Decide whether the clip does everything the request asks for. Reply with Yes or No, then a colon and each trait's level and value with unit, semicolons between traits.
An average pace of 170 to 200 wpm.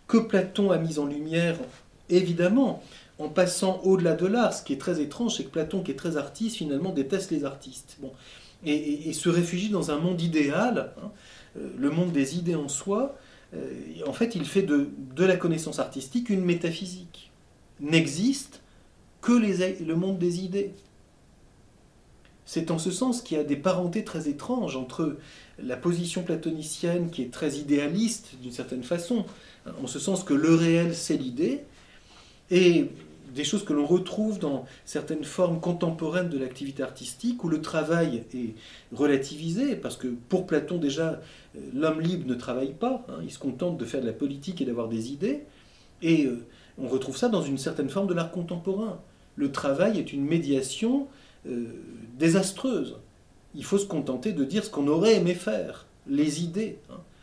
Yes: average, 175 wpm